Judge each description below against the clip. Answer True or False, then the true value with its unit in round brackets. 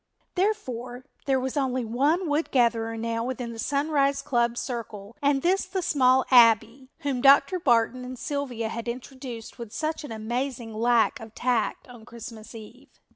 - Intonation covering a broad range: False (3.3 semitones)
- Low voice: False (250 Hz)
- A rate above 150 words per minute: True (160 wpm)